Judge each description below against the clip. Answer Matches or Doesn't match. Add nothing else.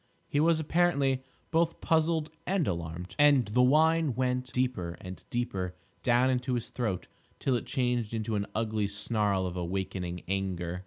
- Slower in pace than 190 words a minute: Matches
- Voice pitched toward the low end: Matches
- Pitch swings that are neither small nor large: Doesn't match